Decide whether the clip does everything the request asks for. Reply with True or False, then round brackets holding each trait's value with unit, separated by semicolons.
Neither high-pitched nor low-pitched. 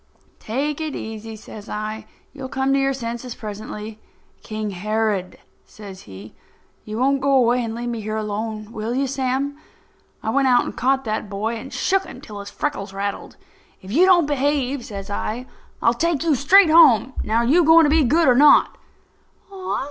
False (240 Hz)